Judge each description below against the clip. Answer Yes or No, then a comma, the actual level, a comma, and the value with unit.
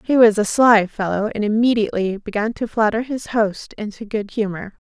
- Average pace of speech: Yes, average, 185 wpm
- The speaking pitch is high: Yes, high, 215 Hz